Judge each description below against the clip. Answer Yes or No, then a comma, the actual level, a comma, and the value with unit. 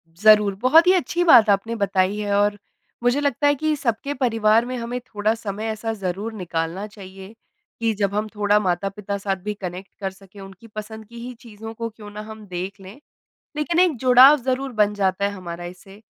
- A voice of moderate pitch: No, high, 210 Hz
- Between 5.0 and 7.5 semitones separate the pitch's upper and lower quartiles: No, average, 3.0 semitones